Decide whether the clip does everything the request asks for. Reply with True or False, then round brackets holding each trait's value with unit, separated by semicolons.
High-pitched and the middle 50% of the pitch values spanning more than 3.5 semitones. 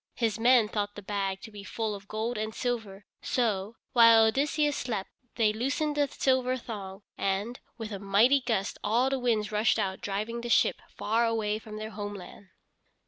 False (220 Hz; 2.8 semitones)